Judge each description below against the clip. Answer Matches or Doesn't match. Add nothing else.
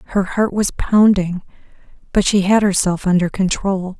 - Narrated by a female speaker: Matches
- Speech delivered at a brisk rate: Doesn't match